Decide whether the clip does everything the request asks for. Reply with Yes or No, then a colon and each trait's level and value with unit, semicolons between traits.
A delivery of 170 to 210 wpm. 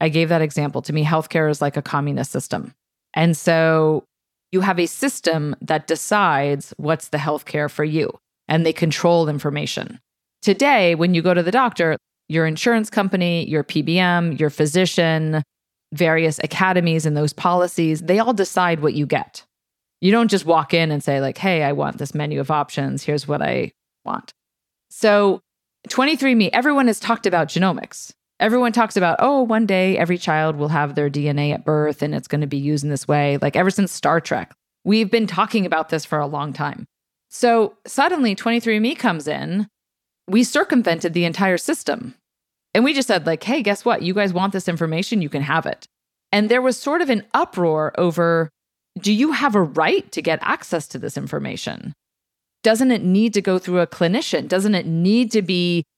Yes: average, 190 wpm